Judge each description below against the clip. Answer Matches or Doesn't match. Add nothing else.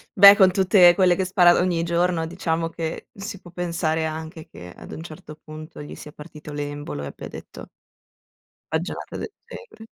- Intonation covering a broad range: Doesn't match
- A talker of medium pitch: Matches